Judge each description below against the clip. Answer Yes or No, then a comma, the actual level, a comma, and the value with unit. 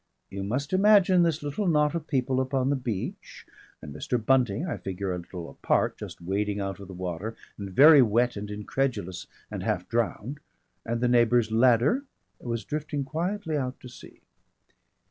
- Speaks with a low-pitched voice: Yes, low, 125 Hz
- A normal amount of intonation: No, wide, 6.2 semitones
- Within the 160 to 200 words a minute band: Yes, average, 170 wpm